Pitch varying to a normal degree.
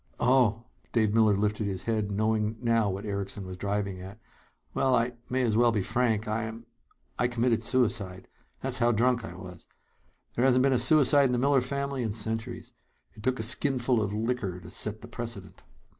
Yes: average, 3.2 semitones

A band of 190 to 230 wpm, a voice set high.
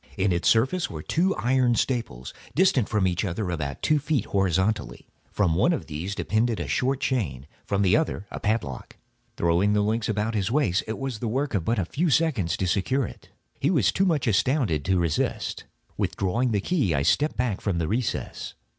No: average, 200 wpm; low, 105 Hz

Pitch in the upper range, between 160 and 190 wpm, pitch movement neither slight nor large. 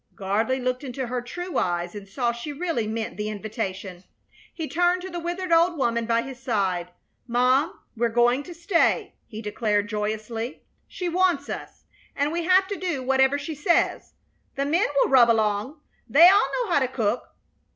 No: very high, 255 Hz; average, 180 wpm; wide, 7.1 semitones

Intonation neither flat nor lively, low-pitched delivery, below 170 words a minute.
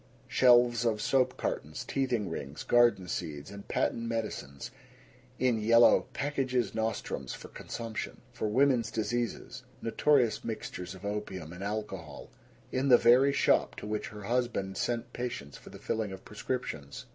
Yes: average, 3.9 semitones; low, 110 Hz; average, 145 wpm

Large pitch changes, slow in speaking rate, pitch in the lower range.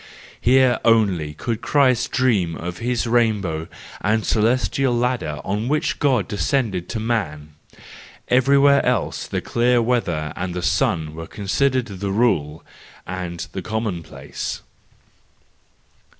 Yes: wide, 5.7 semitones; slow, 120 wpm; low, 110 Hz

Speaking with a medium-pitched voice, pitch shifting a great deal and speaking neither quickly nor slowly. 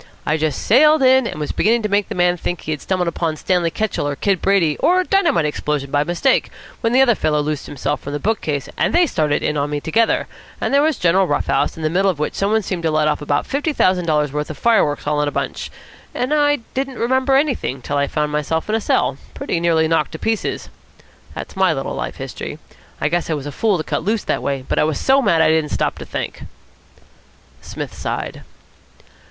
No: medium, 170 Hz; wide, 7.1 semitones; fast, 240 wpm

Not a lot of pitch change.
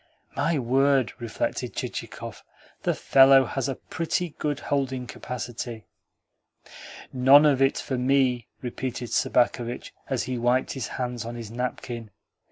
Yes: narrow, 2.0 semitones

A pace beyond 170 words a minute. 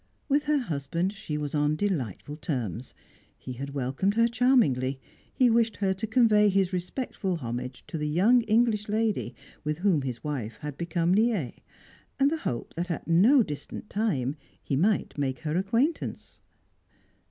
No: average, 160 wpm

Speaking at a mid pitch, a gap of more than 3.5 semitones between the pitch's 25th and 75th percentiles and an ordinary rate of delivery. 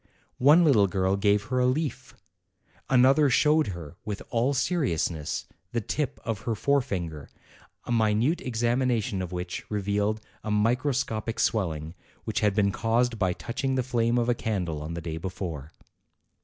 No: low, 110 Hz; average, 5.1 semitones; average, 165 wpm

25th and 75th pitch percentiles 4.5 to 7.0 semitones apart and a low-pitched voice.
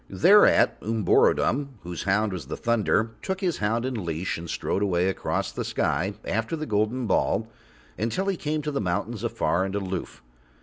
Yes: wide, 5.6 semitones; low, 105 Hz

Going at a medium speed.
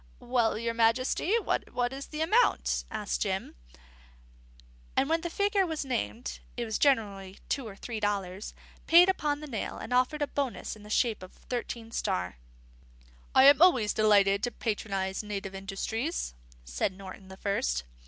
Yes: average, 160 wpm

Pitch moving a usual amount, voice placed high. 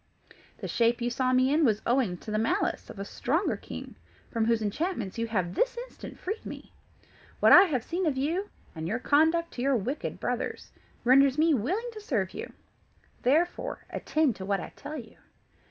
No: wide, 6.4 semitones; very high, 260 Hz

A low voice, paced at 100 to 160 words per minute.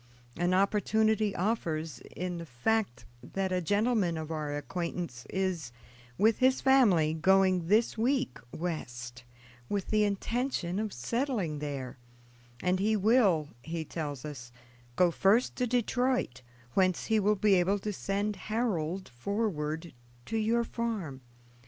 No: high, 190 Hz; slow, 135 wpm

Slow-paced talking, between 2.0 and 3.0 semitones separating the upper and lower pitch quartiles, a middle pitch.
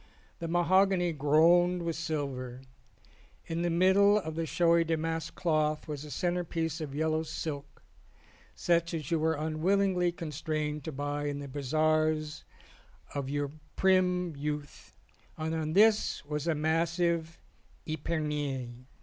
Yes: slow, 130 wpm; narrow, 2.4 semitones; medium, 160 Hz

